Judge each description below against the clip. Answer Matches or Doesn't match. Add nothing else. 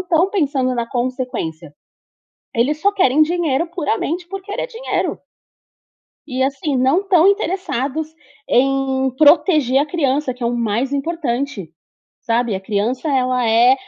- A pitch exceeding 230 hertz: Matches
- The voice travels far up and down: Doesn't match